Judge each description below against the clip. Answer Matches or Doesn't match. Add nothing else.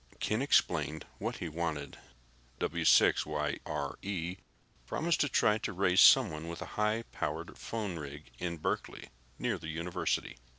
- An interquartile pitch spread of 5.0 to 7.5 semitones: Matches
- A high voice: Doesn't match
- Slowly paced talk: Matches